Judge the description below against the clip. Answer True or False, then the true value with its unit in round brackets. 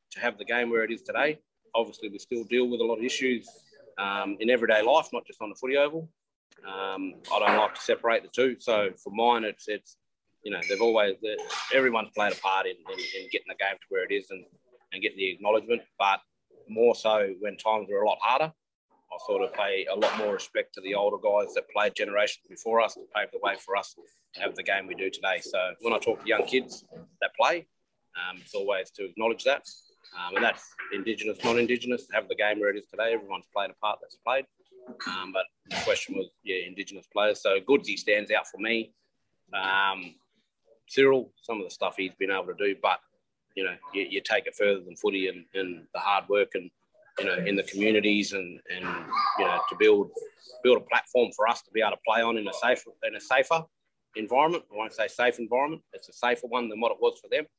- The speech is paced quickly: True (230 wpm)